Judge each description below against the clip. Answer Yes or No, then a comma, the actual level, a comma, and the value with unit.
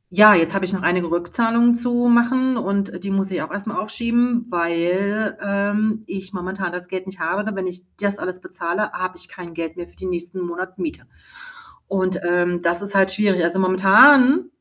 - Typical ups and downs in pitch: Yes, average, 3.1 semitones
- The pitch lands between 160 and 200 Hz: Yes, high, 190 Hz